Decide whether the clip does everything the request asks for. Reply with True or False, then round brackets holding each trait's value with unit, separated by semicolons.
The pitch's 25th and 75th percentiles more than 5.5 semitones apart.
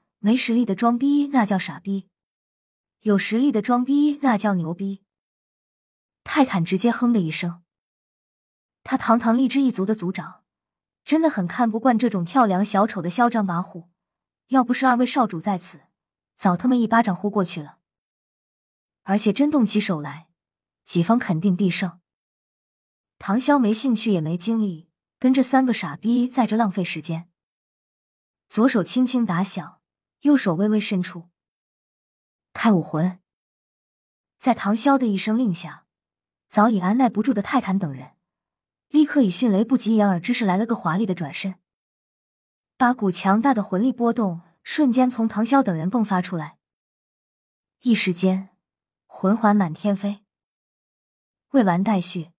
False (5.2 semitones)